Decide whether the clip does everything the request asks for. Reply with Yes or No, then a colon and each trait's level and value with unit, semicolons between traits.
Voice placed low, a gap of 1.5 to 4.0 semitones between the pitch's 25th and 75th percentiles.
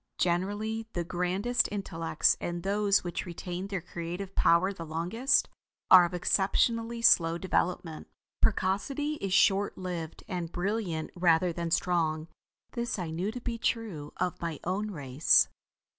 No: medium, 180 Hz; average, 3.3 semitones